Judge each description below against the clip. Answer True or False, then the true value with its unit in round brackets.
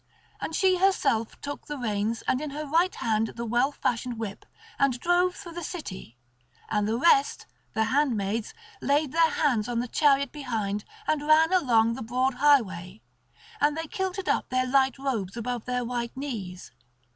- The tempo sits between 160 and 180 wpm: True (170 wpm)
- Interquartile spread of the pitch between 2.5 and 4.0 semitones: False (5.0 semitones)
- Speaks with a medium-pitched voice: False (255 Hz)